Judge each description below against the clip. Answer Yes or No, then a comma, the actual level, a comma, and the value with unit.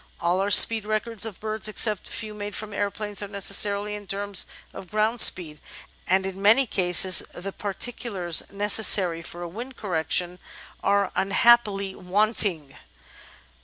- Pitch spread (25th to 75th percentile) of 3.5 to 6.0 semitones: No, narrow, 2.4 semitones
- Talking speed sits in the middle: Yes, average, 150 wpm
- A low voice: No, high, 200 Hz